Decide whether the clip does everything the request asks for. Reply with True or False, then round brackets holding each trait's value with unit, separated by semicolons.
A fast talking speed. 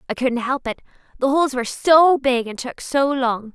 True (220 wpm)